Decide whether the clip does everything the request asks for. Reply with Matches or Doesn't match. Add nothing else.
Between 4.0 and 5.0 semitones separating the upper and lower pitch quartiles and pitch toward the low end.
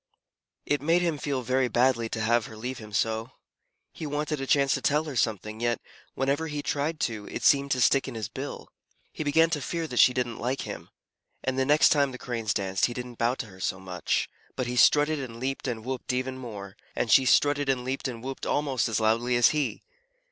Doesn't match